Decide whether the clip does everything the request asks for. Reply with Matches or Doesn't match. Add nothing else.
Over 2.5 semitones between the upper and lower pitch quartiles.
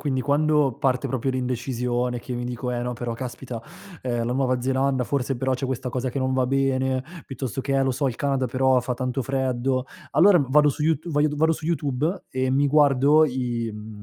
Doesn't match